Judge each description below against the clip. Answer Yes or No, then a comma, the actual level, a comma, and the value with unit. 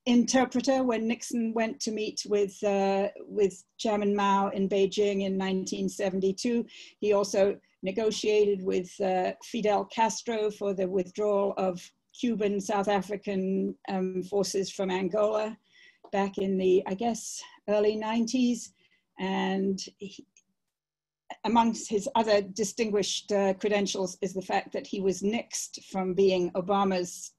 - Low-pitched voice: No, high, 200 Hz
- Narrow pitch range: Yes, narrow, 2.2 semitones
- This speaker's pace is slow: Yes, slow, 125 wpm